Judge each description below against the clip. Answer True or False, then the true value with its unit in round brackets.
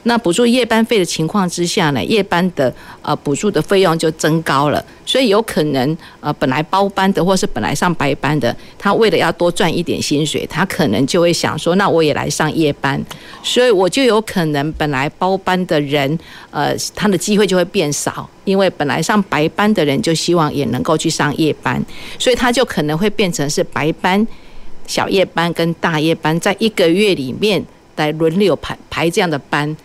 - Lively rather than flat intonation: False (4.3 semitones)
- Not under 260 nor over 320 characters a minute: True (285 characters per minute)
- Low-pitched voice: False (165 Hz)